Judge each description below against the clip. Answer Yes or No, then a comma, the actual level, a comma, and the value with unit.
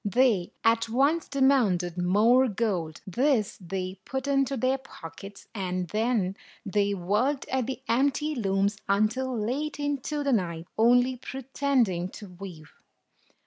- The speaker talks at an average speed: No, slow, 130 wpm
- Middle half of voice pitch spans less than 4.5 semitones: No, wide, 5.6 semitones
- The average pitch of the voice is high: Yes, high, 225 Hz